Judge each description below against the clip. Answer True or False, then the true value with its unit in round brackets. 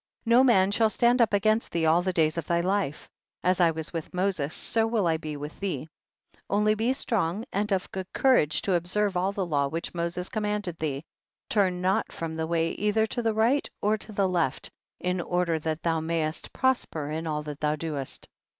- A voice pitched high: False (180 Hz)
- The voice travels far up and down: False (4.6 semitones)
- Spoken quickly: True (210 wpm)